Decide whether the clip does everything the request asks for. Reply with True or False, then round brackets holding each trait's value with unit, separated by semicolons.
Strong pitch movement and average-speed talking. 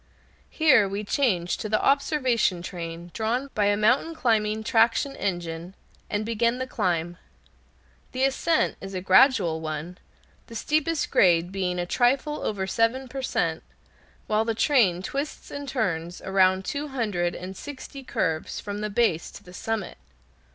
True (6.3 semitones; 150 wpm)